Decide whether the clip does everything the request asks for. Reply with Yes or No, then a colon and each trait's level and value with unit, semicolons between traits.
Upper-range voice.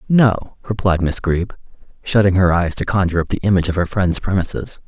No: very low, 95 Hz